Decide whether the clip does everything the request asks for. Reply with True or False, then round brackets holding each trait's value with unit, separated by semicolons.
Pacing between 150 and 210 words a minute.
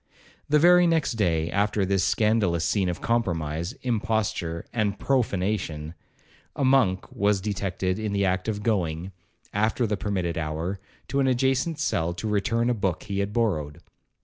True (155 wpm)